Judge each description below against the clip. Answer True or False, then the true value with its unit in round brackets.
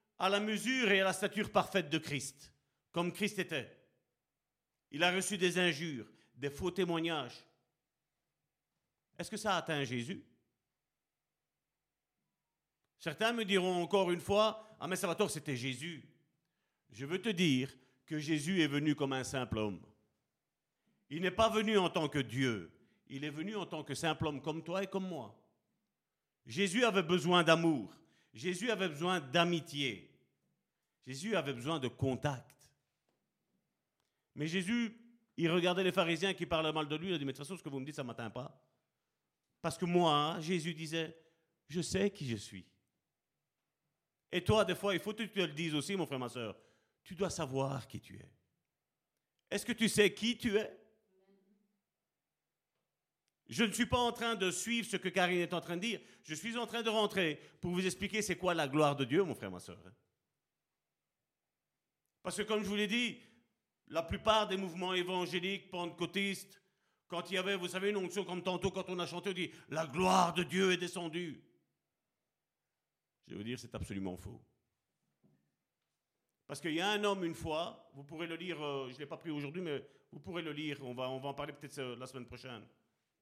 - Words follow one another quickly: False (185 wpm)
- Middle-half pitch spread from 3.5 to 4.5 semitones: False (5.0 semitones)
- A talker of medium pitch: True (175 Hz)